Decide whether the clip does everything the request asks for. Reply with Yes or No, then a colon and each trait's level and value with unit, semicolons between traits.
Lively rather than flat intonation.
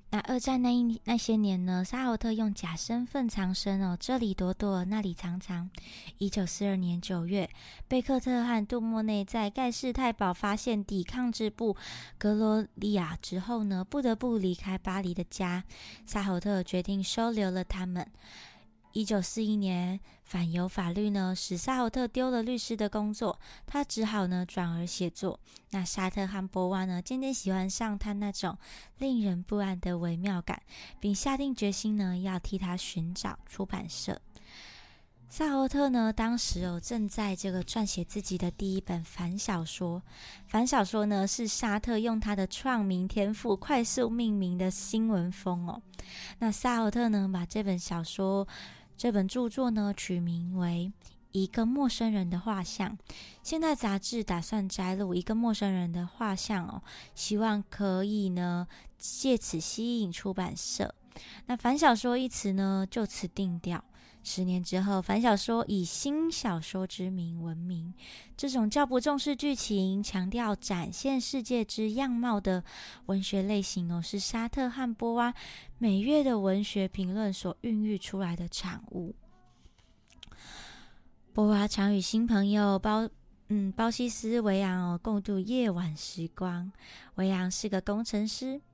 No: average, 3.6 semitones